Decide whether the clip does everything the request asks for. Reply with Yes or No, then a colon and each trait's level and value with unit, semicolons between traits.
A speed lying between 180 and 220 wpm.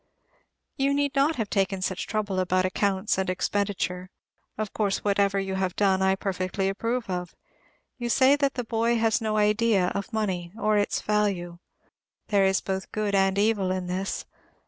No: average, 170 wpm